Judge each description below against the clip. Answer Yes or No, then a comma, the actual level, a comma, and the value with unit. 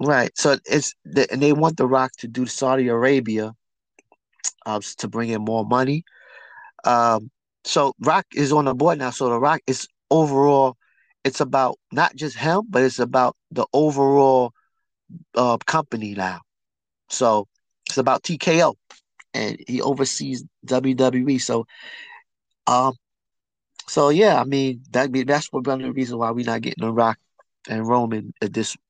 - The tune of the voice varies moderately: Yes, average, 3.6 semitones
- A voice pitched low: Yes, low, 130 Hz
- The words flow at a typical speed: Yes, average, 155 wpm